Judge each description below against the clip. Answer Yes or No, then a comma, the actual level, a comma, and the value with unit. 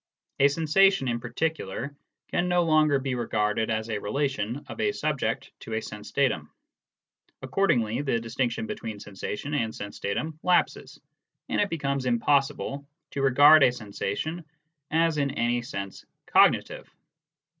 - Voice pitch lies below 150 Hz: Yes, low, 135 Hz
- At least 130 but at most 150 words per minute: Yes, average, 145 wpm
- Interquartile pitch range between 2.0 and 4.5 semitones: No, average, 5.3 semitones